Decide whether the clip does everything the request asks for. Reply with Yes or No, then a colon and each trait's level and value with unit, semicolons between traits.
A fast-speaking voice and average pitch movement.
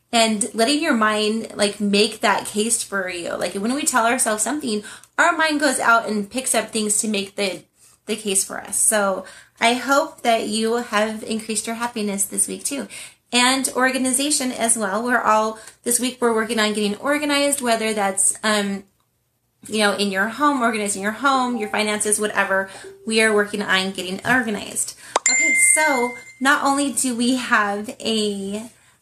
No: average, 175 wpm; average, 3.4 semitones